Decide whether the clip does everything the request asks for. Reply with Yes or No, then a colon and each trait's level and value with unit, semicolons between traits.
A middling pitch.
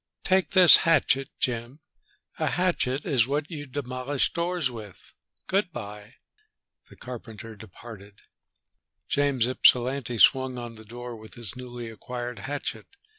No: low, 125 Hz